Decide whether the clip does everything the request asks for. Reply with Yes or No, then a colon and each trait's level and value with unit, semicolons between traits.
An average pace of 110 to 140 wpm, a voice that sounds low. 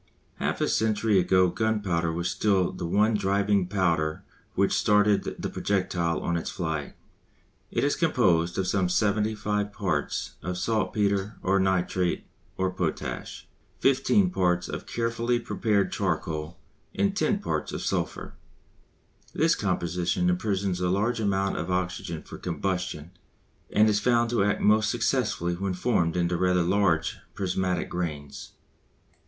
Yes: slow, 135 wpm; very low, 95 Hz